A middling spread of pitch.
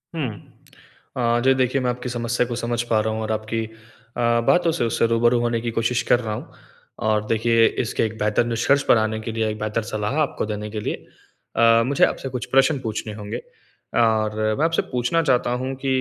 No: narrow, 2.2 semitones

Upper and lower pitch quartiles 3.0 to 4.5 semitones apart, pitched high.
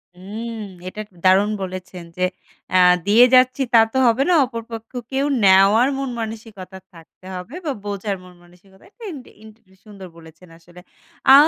Yes: average, 3.9 semitones; high, 205 Hz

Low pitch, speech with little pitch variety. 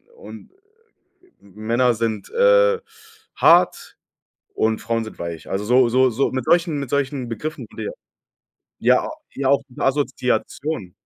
No: low, 130 Hz; average, 5.1 semitones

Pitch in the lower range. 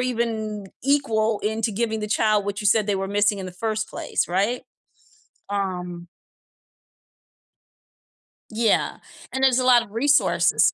No: high, 215 Hz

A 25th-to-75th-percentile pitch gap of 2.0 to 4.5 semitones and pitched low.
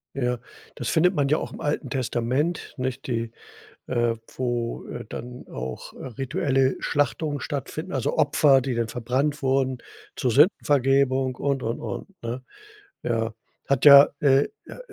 Yes: average, 2.7 semitones; low, 130 Hz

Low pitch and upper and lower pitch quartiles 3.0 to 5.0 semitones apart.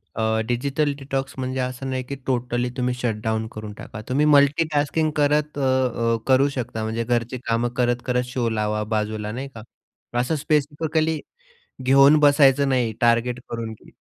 Yes: low, 125 Hz; average, 3.4 semitones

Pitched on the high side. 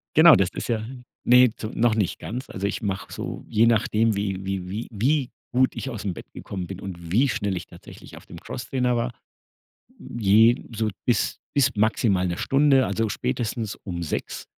No: low, 110 Hz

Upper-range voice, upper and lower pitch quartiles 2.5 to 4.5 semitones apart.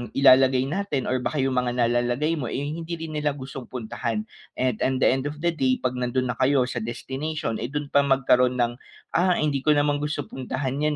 No: low, 135 Hz; average, 2.8 semitones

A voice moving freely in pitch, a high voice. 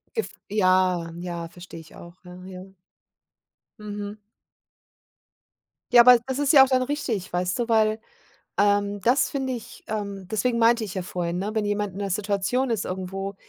No: average, 4.1 semitones; high, 205 Hz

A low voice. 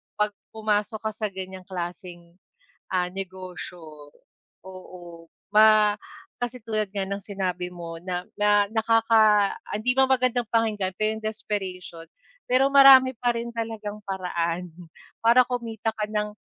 No: high, 210 Hz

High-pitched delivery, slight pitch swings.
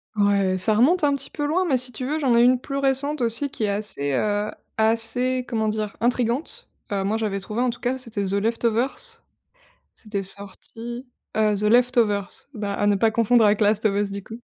No: high, 225 Hz; average, 3.6 semitones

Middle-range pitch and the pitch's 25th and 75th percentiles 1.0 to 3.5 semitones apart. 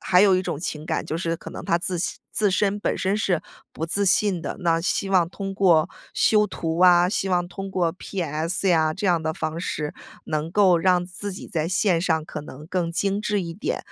Yes: medium, 180 Hz; average, 2.8 semitones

